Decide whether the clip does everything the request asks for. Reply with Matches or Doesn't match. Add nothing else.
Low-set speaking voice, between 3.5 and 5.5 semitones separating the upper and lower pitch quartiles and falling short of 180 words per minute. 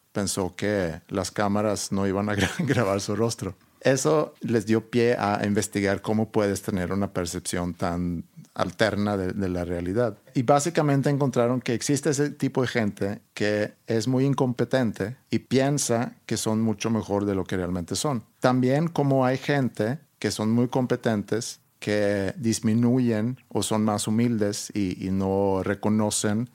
Matches